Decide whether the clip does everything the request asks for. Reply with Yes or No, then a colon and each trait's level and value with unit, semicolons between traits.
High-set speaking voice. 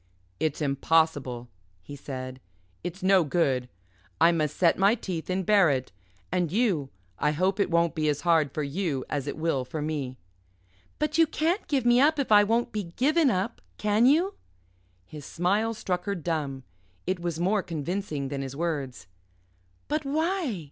No: medium, 170 Hz